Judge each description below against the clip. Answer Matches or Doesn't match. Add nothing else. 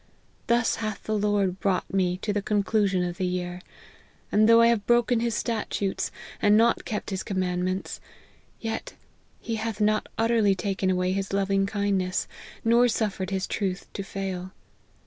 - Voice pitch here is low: Doesn't match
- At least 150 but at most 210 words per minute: Matches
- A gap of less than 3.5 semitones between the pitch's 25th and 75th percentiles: Matches